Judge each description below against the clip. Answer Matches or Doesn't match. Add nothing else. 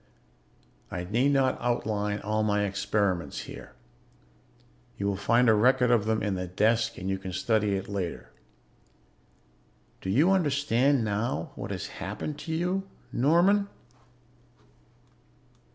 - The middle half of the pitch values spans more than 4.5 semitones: Matches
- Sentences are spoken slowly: Matches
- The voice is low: Matches